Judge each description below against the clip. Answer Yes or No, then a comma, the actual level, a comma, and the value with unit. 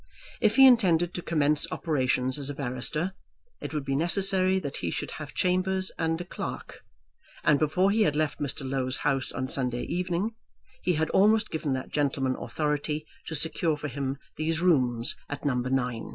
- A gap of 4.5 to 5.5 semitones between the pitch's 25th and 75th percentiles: Yes, average, 4.8 semitones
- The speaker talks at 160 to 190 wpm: Yes, average, 175 wpm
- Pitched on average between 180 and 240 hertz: No, medium, 155 Hz